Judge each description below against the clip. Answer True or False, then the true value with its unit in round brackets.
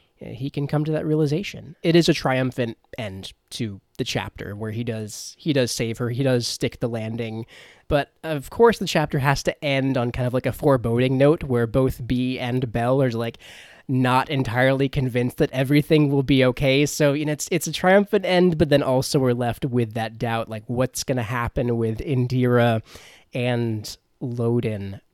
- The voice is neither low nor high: False (130 Hz)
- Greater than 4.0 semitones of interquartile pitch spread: False (3.6 semitones)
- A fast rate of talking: False (195 wpm)